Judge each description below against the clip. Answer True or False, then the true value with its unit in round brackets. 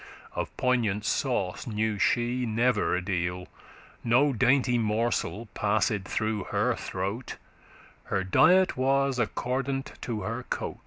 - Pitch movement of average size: True (3.4 semitones)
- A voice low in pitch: True (115 Hz)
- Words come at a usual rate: False (125 wpm)